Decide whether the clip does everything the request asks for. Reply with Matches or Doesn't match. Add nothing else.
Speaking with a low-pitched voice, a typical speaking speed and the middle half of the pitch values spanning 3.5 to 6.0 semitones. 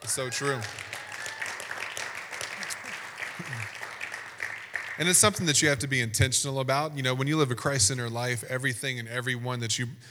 Doesn't match